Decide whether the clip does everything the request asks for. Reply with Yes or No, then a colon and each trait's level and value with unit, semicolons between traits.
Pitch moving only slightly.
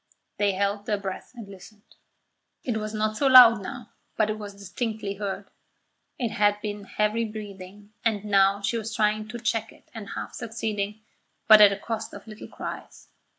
Yes: narrow, 1.6 semitones